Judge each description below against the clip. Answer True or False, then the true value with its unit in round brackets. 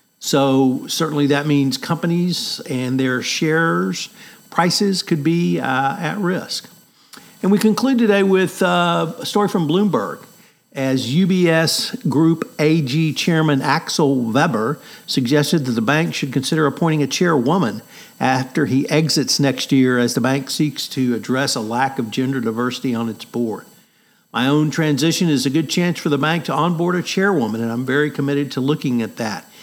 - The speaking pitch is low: False (155 Hz)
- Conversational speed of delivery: True (165 wpm)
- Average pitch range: True (4.6 semitones)